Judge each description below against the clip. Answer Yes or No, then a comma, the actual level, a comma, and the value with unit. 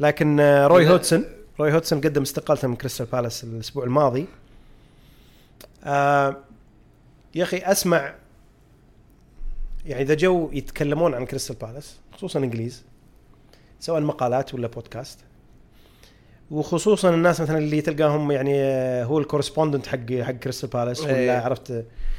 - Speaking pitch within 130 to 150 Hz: Yes, medium, 140 Hz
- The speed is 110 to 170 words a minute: Yes, average, 115 wpm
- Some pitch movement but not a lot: Yes, average, 3.7 semitones